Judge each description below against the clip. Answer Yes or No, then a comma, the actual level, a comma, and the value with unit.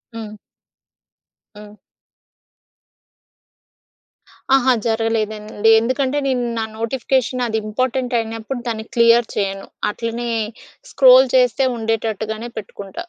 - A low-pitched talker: No, high, 230 Hz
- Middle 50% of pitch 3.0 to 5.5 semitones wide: No, narrow, 2.6 semitones